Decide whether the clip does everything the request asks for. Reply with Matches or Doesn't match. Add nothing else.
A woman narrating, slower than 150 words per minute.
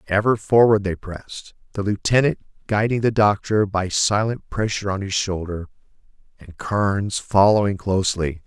Doesn't match